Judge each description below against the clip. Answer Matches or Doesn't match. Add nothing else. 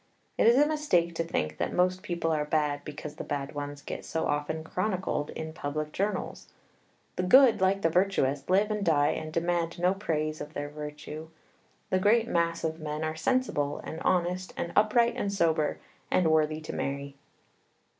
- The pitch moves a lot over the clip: Doesn't match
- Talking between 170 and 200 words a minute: Matches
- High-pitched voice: Doesn't match